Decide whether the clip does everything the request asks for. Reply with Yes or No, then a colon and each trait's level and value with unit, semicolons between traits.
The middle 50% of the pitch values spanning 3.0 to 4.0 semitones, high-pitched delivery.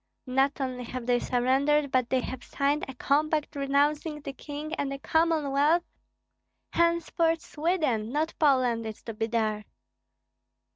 Yes: average, 3.3 semitones; very high, 280 Hz